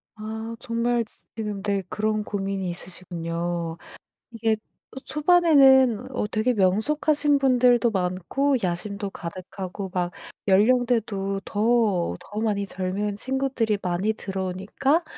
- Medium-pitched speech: No, high, 210 Hz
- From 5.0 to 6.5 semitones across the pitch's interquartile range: No, average, 4.3 semitones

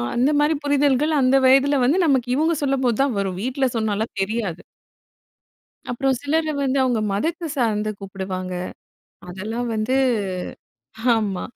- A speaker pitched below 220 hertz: No, very high, 250 Hz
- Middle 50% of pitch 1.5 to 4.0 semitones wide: No, average, 4.8 semitones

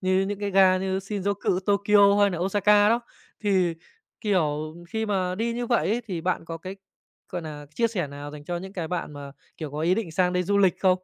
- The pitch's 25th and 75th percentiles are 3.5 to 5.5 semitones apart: No, average, 3.1 semitones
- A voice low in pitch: No, medium, 185 Hz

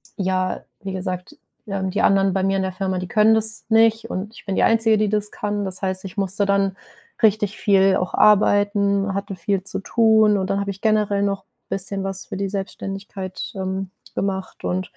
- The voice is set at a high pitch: Yes, high, 195 Hz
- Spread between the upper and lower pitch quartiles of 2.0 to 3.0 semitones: No, narrow, 1.5 semitones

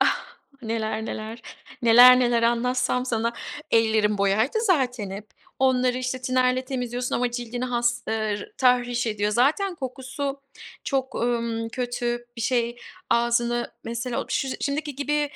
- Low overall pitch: No, high, 245 Hz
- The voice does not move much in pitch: Yes, narrow, 1.7 semitones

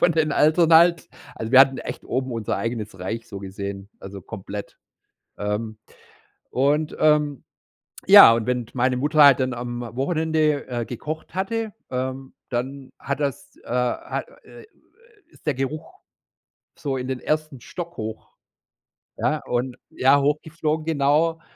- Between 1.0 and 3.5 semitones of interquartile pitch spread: No, average, 4.5 semitones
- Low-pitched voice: Yes, low, 130 Hz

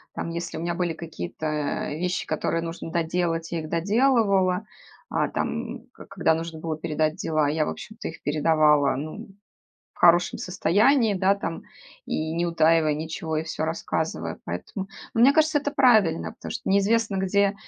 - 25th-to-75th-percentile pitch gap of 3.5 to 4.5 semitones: Yes, average, 4.0 semitones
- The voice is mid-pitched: Yes, medium, 170 Hz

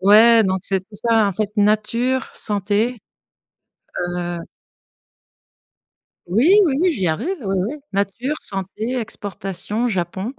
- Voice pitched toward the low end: No, high, 210 Hz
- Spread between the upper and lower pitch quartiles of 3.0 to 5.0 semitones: Yes, average, 3.5 semitones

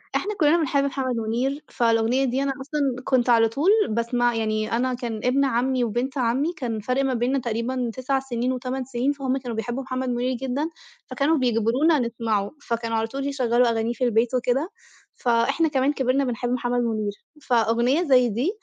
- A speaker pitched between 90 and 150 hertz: No, very high, 250 Hz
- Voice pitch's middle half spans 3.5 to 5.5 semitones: No, narrow, 2.5 semitones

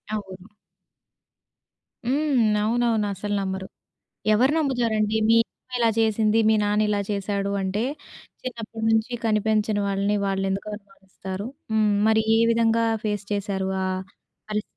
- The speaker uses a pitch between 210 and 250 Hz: Yes, high, 215 Hz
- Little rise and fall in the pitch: Yes, narrow, 2.1 semitones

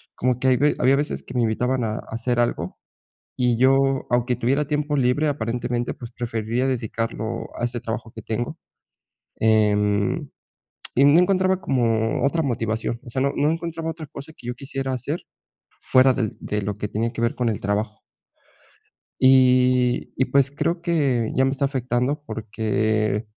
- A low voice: Yes, low, 125 Hz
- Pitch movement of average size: Yes, average, 3.4 semitones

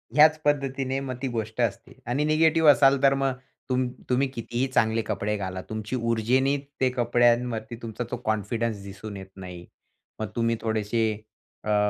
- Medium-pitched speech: No, low, 115 Hz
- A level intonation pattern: No, average, 3.4 semitones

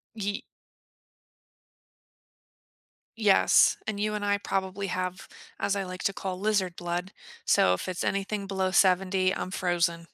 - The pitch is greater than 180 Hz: Yes, high, 190 Hz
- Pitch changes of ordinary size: No, narrow, 1.6 semitones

